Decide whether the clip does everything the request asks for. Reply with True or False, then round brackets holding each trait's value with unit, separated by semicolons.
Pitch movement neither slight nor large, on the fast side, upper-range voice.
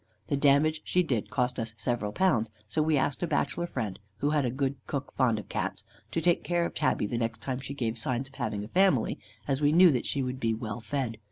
False (4.5 semitones; 245 wpm; 130 Hz)